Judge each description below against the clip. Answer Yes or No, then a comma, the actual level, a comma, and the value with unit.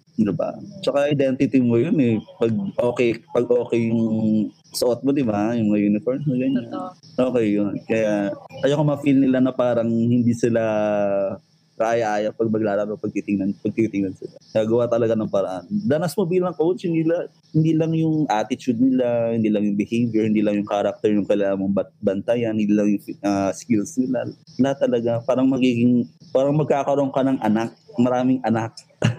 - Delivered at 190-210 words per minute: No, average, 165 wpm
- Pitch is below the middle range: Yes, low, 115 Hz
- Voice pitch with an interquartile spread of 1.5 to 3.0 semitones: No, average, 3.9 semitones